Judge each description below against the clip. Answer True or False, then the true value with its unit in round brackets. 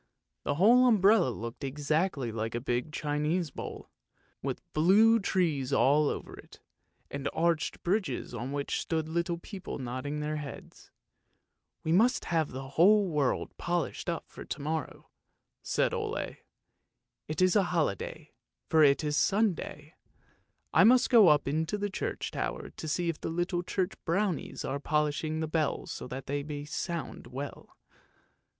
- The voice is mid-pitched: True (155 Hz)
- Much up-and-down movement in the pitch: False (4.0 semitones)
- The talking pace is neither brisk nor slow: True (160 wpm)